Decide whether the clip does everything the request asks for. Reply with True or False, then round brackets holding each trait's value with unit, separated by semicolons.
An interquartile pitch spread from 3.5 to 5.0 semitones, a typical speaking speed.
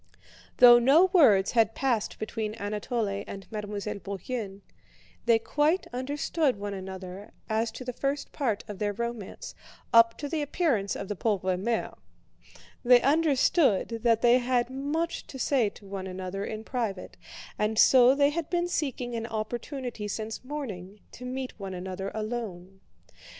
True (4.6 semitones; 150 wpm)